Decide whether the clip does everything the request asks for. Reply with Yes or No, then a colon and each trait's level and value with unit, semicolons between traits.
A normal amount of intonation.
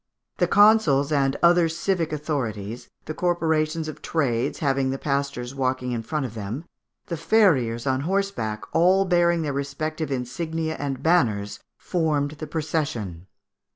Yes: average, 4.3 semitones